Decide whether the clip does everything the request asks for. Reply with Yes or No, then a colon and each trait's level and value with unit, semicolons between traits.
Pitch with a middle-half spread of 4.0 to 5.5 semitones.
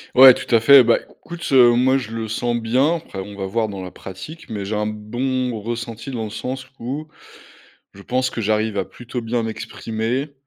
No: average, 3.2 semitones